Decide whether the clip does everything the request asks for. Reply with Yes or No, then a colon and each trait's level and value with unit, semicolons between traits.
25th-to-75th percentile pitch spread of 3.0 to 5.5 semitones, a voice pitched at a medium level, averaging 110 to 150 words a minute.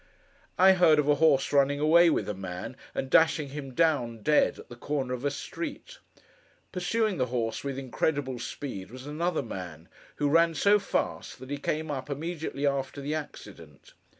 No: average, 3.8 semitones; medium, 145 Hz; average, 180 wpm